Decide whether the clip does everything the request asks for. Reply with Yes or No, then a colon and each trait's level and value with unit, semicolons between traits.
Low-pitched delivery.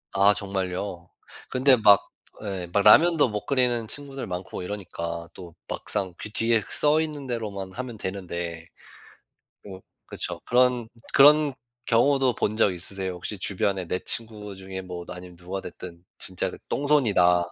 Yes: low, 100 Hz